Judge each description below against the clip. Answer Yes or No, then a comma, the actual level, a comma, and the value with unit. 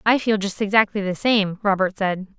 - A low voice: No, high, 200 Hz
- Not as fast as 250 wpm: Yes, average, 200 wpm